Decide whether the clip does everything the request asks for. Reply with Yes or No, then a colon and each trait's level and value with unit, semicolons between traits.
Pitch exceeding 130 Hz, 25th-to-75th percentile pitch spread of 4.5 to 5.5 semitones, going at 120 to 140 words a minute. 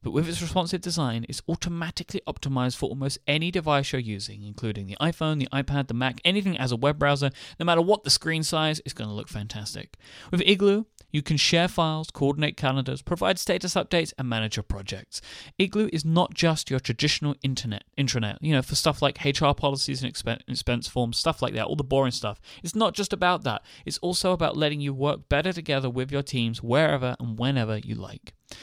No: medium, 140 Hz; average, 4.9 semitones; fast, 205 wpm